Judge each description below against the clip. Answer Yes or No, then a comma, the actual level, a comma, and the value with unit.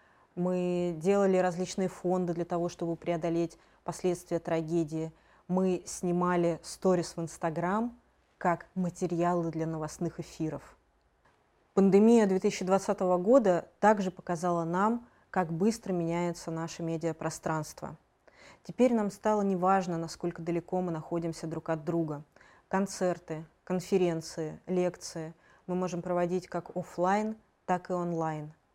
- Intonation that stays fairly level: Yes, narrow, 1.9 semitones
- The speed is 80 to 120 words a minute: Yes, slow, 110 wpm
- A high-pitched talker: No, medium, 175 Hz